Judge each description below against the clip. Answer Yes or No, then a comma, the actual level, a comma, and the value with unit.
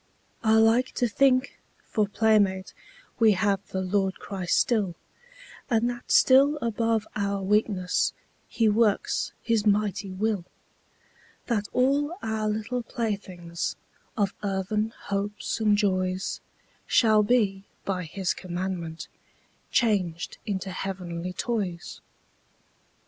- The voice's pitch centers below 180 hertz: No, high, 205 Hz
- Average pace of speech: No, slow, 110 wpm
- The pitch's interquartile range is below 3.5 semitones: Yes, average, 2.9 semitones